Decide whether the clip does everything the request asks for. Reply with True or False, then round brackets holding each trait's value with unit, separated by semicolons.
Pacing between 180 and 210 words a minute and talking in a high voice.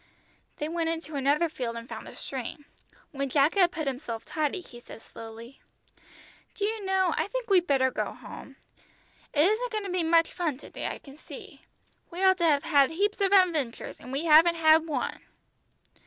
True (195 wpm; 320 Hz)